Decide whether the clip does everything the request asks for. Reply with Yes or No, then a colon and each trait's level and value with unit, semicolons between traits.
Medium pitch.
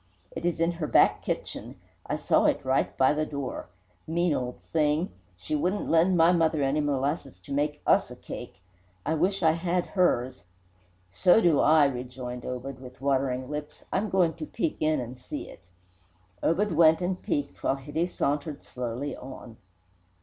Yes: medium, 150 Hz